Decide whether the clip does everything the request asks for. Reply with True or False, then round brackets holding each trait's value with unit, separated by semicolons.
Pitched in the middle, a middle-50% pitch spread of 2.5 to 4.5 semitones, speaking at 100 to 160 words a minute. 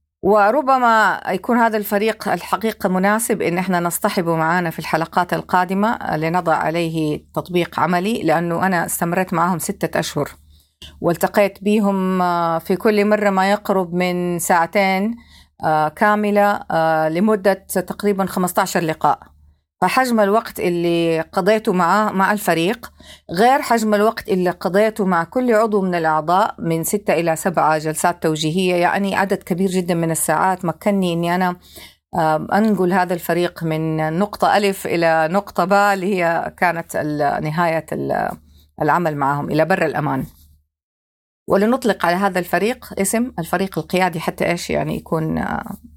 True (180 Hz; 3.7 semitones; 130 wpm)